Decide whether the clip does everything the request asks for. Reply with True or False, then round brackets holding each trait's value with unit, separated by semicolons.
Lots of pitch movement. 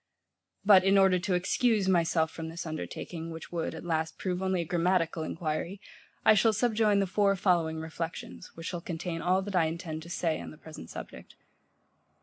False (2.8 semitones)